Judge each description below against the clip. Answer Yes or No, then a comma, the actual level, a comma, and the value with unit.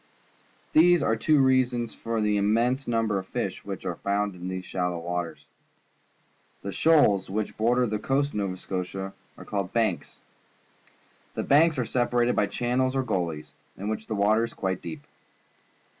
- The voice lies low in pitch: Yes, low, 110 Hz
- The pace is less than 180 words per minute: Yes, average, 165 wpm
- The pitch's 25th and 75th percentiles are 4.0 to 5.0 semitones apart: Yes, average, 4.6 semitones